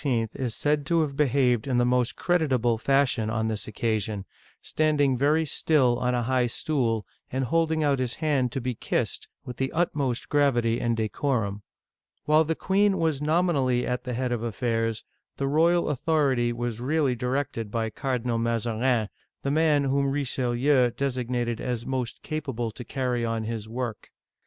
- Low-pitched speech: Yes, low, 125 Hz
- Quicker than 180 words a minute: No, average, 160 wpm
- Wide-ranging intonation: No, average, 3.5 semitones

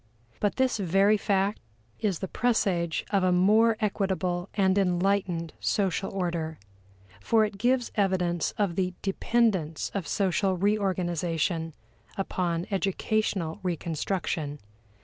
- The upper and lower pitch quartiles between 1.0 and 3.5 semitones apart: Yes, average, 2.8 semitones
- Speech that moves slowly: Yes, slow, 110 wpm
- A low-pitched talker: No, high, 190 Hz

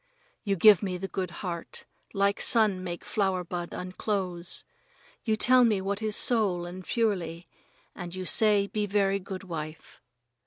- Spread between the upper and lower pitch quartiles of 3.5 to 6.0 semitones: No, average, 2.7 semitones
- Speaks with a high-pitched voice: Yes, high, 195 Hz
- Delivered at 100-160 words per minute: Yes, average, 155 wpm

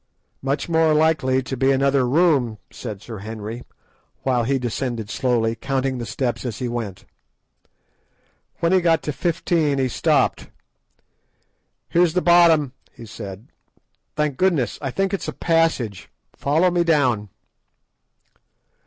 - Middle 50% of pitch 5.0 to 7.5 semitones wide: Yes, wide, 5.4 semitones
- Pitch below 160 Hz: Yes, low, 135 Hz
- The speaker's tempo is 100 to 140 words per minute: Yes, slow, 135 wpm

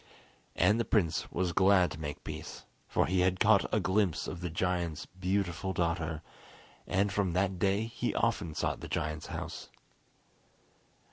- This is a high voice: No, very low, 90 Hz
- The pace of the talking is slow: No, average, 155 wpm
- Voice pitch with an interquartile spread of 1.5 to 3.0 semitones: Yes, narrow, 2.6 semitones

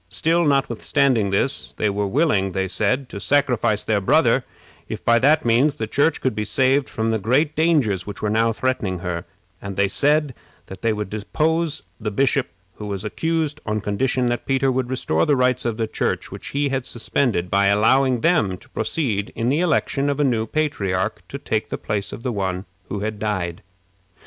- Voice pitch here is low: Yes, low, 115 Hz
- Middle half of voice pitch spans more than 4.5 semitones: Yes, average, 5.2 semitones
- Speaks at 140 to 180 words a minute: No, average, 195 wpm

